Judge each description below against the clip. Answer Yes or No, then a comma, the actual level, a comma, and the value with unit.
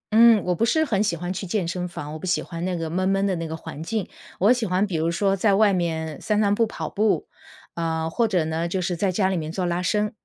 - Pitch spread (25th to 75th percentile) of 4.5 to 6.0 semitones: No, average, 3.8 semitones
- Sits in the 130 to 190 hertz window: Yes, medium, 185 Hz